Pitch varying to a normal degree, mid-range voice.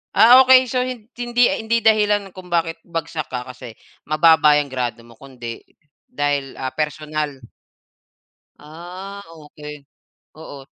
No: wide, 6.6 semitones; medium, 155 Hz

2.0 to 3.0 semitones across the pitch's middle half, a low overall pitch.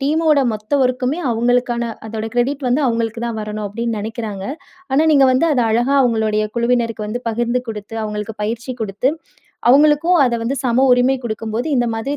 No: narrow, 2.6 semitones; high, 235 Hz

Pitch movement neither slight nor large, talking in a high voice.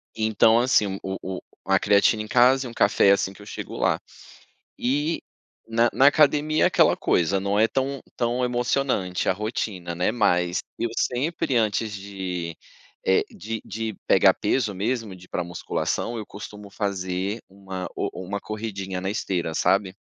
No: average, 3.8 semitones; low, 105 Hz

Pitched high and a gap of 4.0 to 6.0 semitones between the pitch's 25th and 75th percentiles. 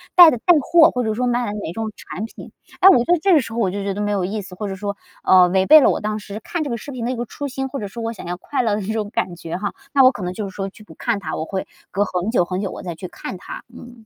Yes: high, 210 Hz; average, 4.4 semitones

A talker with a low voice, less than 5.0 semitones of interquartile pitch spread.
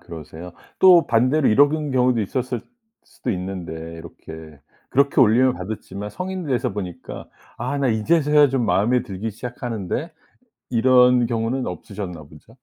No: low, 120 Hz; average, 5.3 semitones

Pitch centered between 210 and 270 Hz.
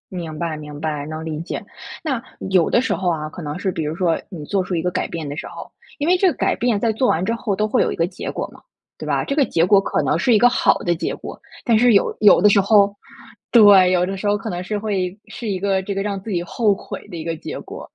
No: high, 190 Hz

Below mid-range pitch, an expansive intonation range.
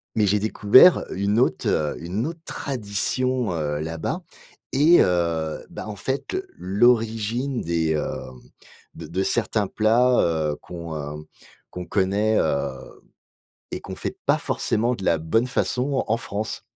Yes: low, 105 Hz; wide, 6.4 semitones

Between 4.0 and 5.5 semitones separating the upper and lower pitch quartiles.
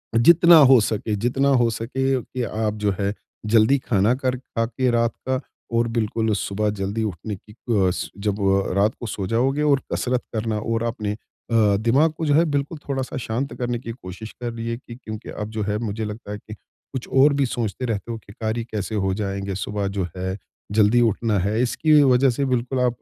No: average, 3.4 semitones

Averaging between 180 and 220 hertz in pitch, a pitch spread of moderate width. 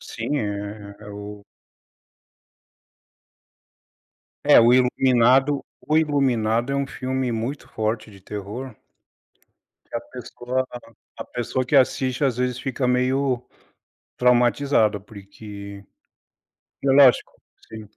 No: low, 125 Hz; average, 3.5 semitones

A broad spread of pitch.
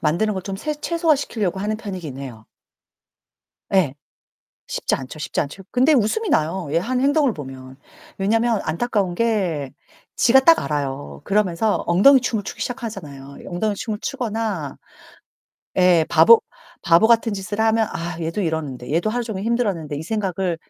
Yes: wide, 6.0 semitones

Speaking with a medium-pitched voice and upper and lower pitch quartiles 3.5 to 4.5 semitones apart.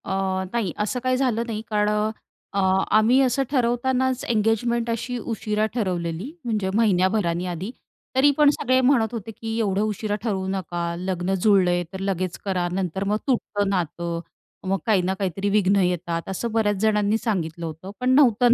No: high, 210 Hz; average, 3.8 semitones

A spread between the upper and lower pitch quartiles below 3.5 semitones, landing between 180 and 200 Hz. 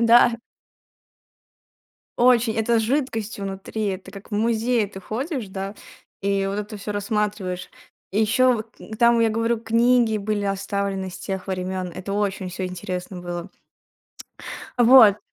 No: average, 3.0 semitones; high, 210 Hz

